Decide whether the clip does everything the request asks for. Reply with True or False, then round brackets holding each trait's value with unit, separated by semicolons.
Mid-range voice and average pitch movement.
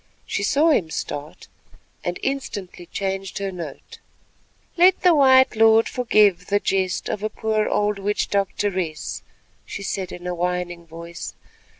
False (195 Hz; 3.6 semitones)